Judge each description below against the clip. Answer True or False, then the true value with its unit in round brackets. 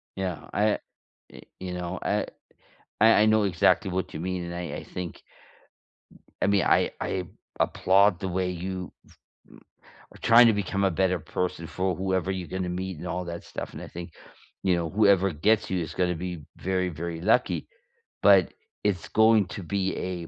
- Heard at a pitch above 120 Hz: False (95 Hz)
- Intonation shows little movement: True (1.9 semitones)